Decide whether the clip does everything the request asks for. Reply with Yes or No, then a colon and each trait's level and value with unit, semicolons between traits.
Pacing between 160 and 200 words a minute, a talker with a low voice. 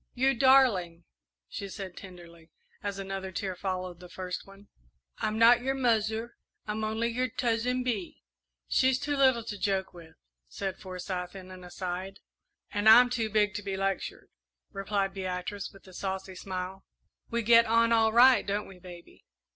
No: average, 165 wpm; high, 200 Hz